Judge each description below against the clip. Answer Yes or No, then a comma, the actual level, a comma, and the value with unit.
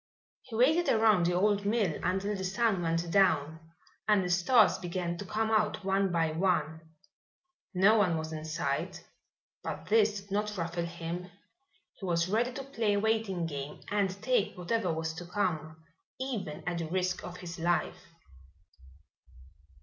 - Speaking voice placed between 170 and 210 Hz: Yes, medium, 185 Hz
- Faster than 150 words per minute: Yes, average, 160 wpm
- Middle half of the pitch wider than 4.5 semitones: No, average, 3.8 semitones